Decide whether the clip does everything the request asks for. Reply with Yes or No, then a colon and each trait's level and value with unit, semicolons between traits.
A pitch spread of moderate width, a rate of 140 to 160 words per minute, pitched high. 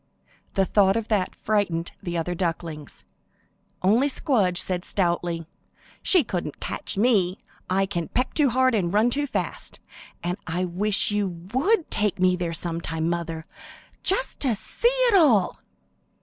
No: wide, 5.7 semitones; average, 150 wpm; high, 195 Hz